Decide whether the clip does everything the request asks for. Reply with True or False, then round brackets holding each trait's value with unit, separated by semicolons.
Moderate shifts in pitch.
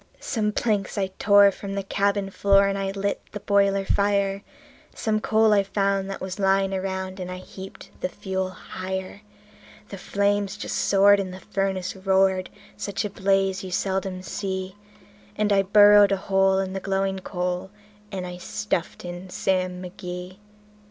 False (1.1 semitones)